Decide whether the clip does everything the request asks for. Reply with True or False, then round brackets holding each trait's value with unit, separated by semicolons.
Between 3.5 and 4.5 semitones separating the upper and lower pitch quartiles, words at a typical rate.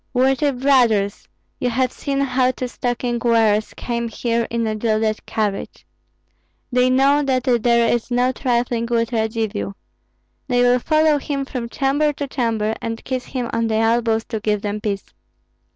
False (2.4 semitones; 160 wpm)